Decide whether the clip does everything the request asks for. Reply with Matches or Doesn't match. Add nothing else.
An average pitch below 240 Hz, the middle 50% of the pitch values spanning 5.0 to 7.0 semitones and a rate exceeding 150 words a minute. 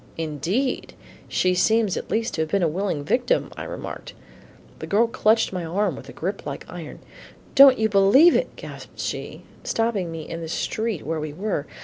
Matches